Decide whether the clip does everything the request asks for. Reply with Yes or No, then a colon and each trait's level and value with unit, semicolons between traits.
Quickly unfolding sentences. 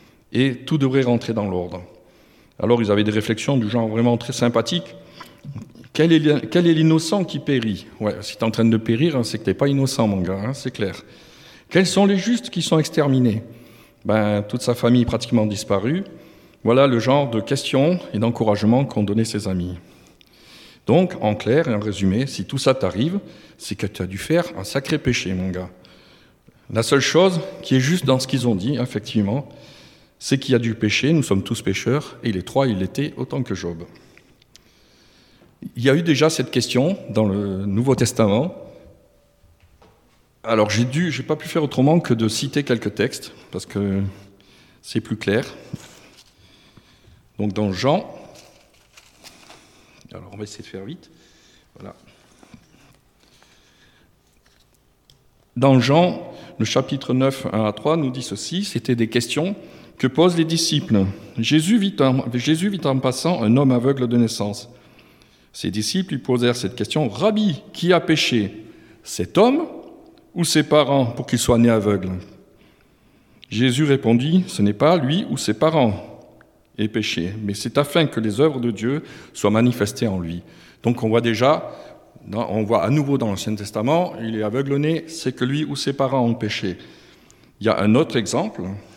No: average, 175 wpm